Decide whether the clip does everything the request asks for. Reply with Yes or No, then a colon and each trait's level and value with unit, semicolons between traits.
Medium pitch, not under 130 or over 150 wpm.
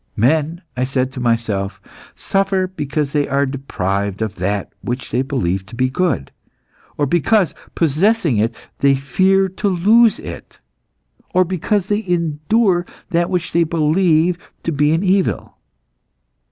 Yes: medium, 155 Hz; average, 140 wpm